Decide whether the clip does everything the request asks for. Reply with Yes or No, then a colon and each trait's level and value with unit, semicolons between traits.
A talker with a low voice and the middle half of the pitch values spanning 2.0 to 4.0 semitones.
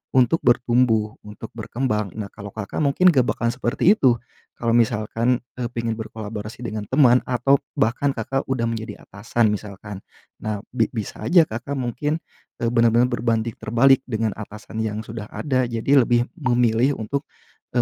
Yes: low, 115 Hz; narrow, 2.6 semitones